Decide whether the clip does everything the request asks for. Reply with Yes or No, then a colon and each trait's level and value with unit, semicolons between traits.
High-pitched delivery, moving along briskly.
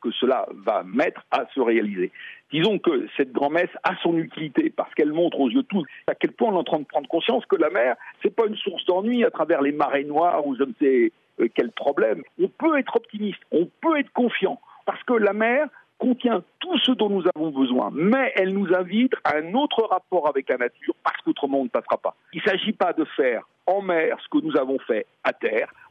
Yes: high, 225 Hz; fast, 235 wpm